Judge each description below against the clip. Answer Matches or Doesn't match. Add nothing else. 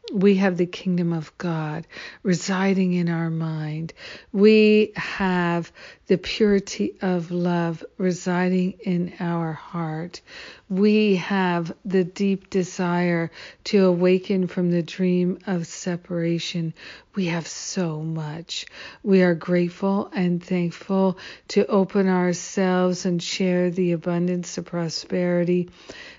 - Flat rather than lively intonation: Matches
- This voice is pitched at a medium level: Matches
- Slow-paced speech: Matches